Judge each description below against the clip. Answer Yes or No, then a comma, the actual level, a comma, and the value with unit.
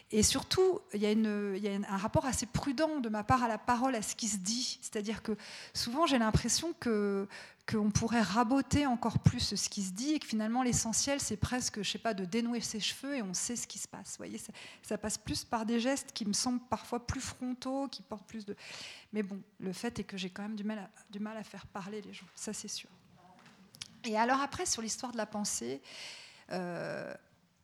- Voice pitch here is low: No, high, 220 Hz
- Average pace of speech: No, fast, 235 wpm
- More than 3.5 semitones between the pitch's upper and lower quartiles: No, average, 3.1 semitones